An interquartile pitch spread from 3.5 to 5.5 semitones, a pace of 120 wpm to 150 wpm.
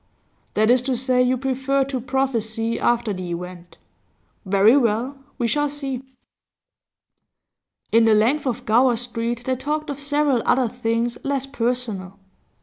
No: average, 3.0 semitones; average, 145 wpm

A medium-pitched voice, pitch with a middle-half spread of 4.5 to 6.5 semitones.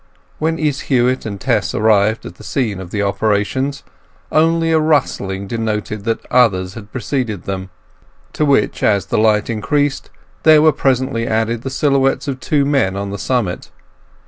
No: low, 115 Hz; average, 5.2 semitones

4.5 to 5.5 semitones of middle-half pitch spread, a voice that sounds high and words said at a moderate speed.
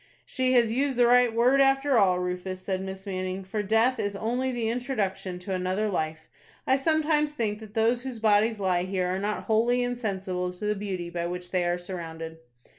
Yes: average, 4.8 semitones; high, 205 Hz; average, 195 wpm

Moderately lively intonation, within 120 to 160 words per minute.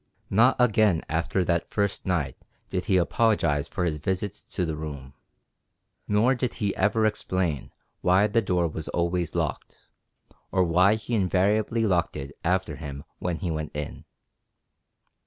Yes: average, 4.4 semitones; average, 150 wpm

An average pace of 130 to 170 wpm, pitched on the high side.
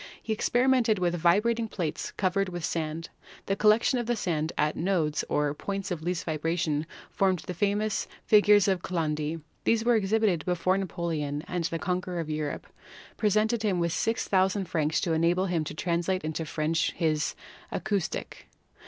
No: average, 160 wpm; medium, 180 Hz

